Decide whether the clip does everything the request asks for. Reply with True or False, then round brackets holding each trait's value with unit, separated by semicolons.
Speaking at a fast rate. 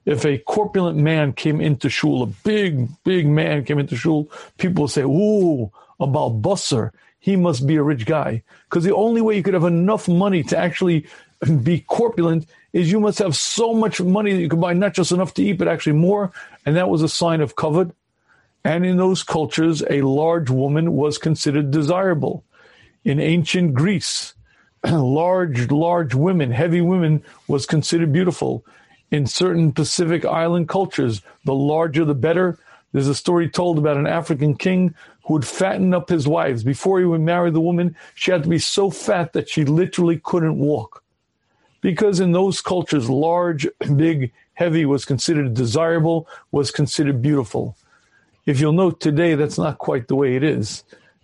False (175 wpm)